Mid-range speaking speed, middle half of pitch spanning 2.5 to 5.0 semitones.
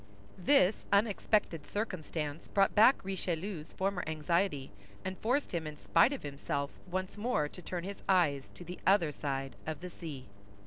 Yes: average, 160 wpm; average, 4.7 semitones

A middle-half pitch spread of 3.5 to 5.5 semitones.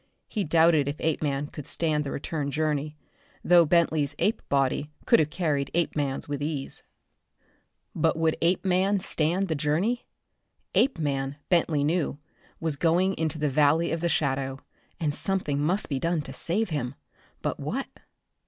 No: average, 2.9 semitones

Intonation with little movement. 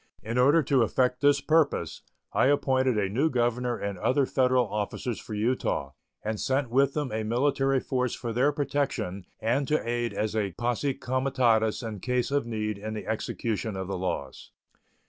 No: average, 3.8 semitones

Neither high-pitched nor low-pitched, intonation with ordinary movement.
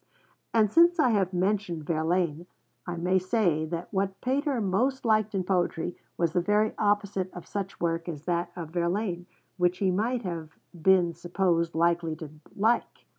Yes: medium, 180 Hz; average, 3.4 semitones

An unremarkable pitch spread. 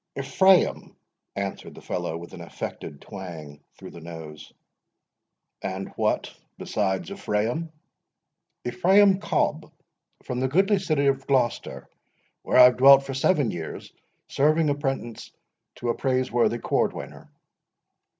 No: wide, 8.0 semitones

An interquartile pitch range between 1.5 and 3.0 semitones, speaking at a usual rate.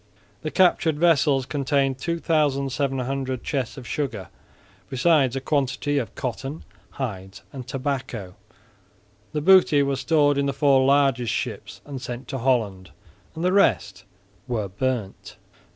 No: narrow, 2.6 semitones; slow, 125 wpm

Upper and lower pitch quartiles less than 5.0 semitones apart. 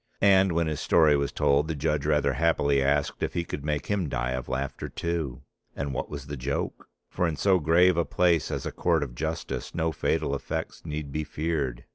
Yes: average, 2.9 semitones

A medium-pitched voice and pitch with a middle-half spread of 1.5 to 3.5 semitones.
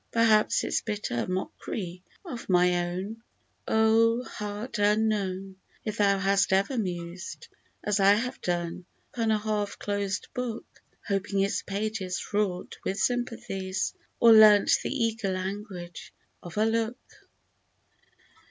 No: high, 205 Hz; average, 2.8 semitones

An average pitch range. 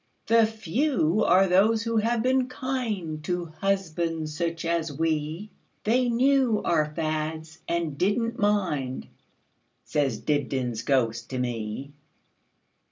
No: wide, 6.5 semitones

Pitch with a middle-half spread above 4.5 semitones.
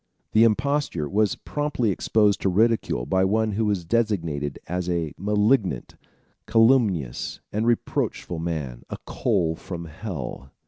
Yes: average, 5.3 semitones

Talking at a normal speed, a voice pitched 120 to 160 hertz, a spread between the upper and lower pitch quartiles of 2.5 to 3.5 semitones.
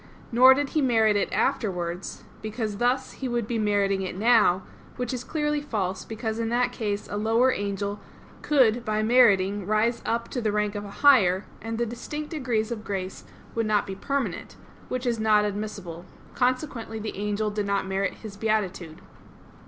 No: average, 175 wpm; high, 215 Hz; average, 3.1 semitones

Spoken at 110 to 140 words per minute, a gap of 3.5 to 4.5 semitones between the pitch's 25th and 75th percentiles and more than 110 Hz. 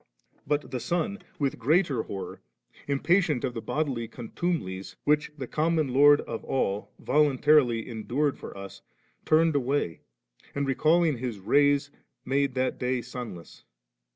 Yes: slow, 135 wpm; average, 3.9 semitones; medium, 140 Hz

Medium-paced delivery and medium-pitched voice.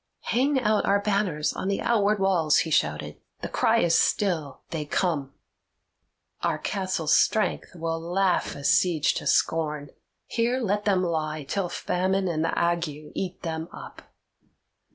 Yes: average, 150 wpm; medium, 175 Hz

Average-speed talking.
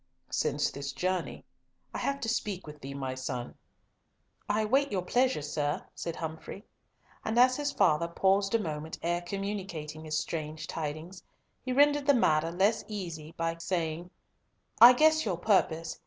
Yes: average, 155 wpm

